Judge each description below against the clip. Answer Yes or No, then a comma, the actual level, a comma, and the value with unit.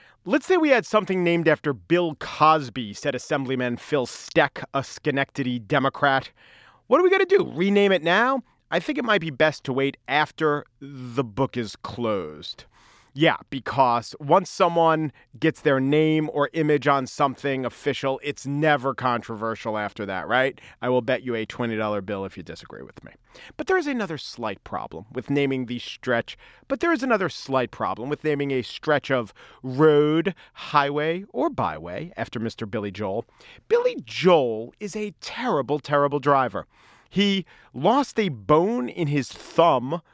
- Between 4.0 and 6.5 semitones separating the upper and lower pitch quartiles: Yes, average, 4.8 semitones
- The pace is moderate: Yes, average, 165 wpm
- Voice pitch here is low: No, medium, 145 Hz